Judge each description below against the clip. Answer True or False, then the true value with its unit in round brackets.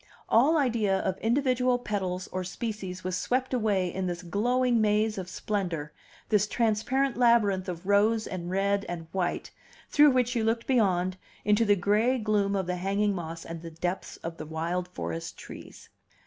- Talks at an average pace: True (170 wpm)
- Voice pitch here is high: True (200 Hz)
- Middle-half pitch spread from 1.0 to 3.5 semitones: False (4.1 semitones)